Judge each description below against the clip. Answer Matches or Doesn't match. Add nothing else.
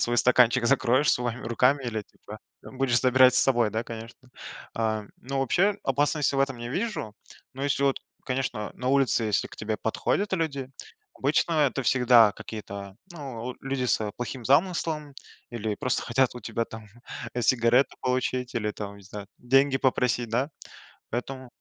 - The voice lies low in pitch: Matches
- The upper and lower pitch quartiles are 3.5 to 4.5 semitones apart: Doesn't match